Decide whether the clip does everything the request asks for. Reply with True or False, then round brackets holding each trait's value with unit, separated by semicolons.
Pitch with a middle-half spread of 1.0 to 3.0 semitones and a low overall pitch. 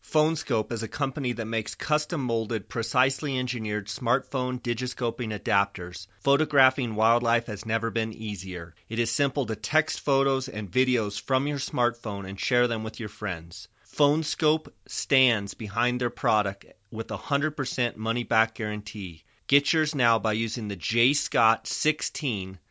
False (3.9 semitones; 115 Hz)